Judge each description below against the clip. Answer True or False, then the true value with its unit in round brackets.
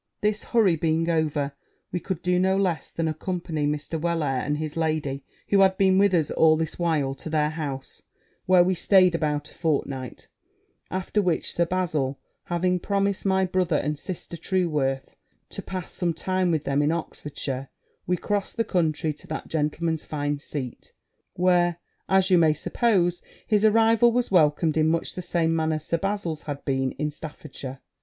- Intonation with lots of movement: False (3.6 semitones)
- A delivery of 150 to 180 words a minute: True (170 wpm)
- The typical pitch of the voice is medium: True (165 Hz)